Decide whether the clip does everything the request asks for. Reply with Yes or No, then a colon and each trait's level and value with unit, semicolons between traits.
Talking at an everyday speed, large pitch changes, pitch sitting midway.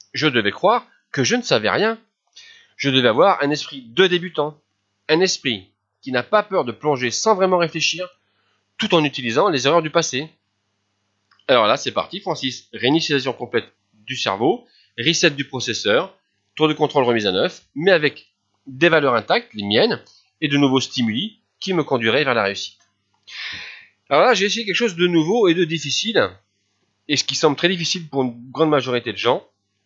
Yes: average, 185 wpm; wide, 6.8 semitones; medium, 145 Hz